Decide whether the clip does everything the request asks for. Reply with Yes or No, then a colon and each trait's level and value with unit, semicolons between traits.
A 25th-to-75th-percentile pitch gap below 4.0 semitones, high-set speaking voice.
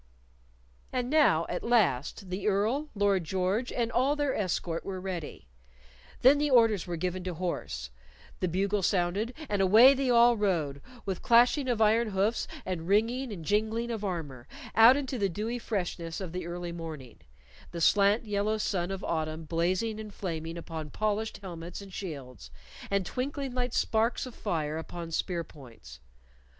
No: average, 5.1 semitones; high, 195 Hz